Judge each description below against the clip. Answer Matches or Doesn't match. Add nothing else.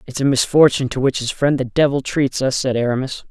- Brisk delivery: Matches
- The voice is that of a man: Matches